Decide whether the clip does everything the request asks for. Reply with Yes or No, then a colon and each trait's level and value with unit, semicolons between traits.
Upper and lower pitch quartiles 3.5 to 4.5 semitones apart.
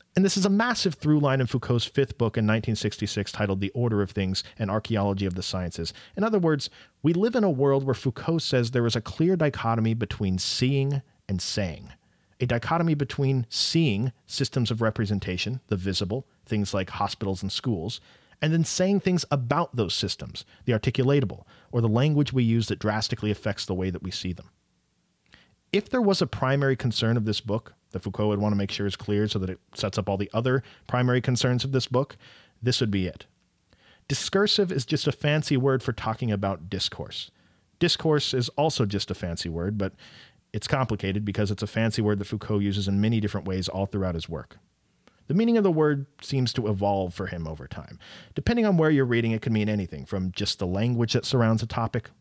No: average, 5.1 semitones